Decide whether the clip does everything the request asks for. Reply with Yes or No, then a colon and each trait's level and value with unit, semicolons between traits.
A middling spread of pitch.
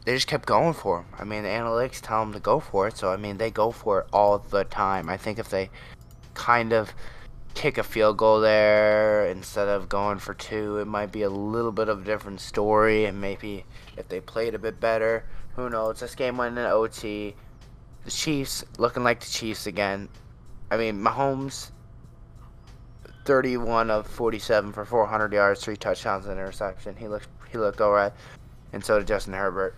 No: narrow, 2.2 semitones